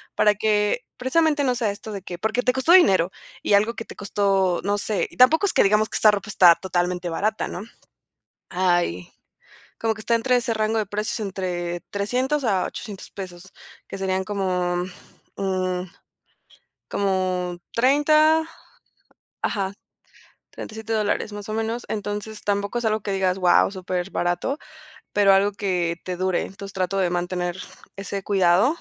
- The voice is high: Yes, high, 200 Hz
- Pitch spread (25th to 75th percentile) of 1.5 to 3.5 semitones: Yes, average, 3.1 semitones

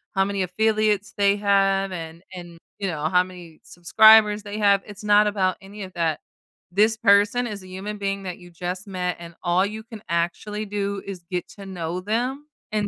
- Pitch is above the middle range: Yes, high, 195 Hz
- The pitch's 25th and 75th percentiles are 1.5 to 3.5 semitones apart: Yes, narrow, 2.6 semitones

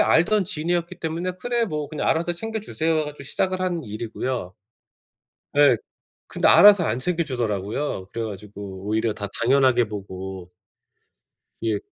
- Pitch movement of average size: No, wide, 8.3 semitones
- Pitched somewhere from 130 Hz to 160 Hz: Yes, medium, 140 Hz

